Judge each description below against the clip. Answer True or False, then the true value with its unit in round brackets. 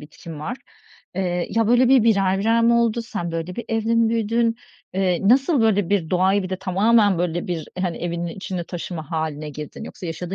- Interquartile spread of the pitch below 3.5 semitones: False (4.8 semitones)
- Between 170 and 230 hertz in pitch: True (190 Hz)